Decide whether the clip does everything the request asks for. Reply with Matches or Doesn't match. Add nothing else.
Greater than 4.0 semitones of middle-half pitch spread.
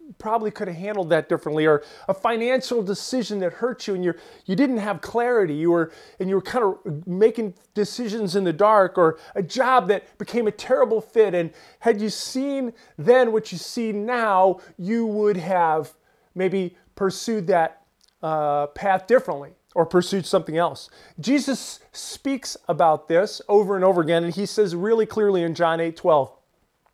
Matches